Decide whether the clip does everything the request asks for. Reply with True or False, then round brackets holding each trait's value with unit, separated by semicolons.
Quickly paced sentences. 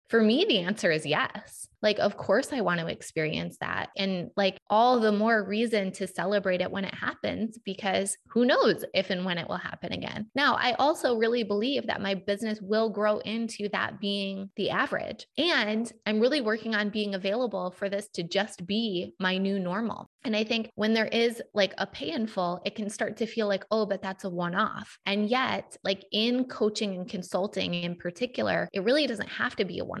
True (210 wpm)